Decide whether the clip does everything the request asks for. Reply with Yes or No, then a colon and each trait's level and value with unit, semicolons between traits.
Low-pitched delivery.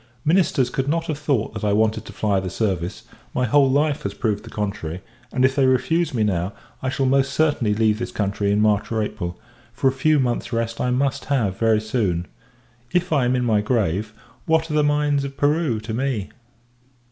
Yes: low, 120 Hz